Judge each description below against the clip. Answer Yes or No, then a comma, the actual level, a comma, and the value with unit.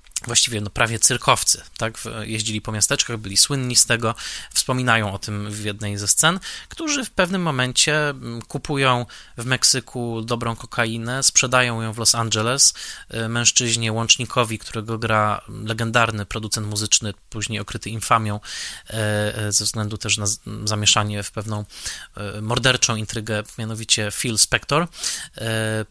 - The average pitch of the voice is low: Yes, low, 115 Hz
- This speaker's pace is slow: No, average, 125 wpm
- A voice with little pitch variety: Yes, narrow, 2.3 semitones